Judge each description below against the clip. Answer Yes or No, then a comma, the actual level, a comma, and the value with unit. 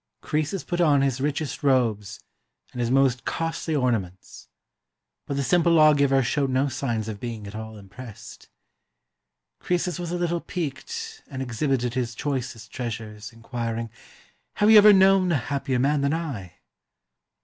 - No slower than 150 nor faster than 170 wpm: Yes, average, 155 wpm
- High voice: No, low, 135 Hz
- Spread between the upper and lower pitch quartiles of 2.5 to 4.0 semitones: No, wide, 5.5 semitones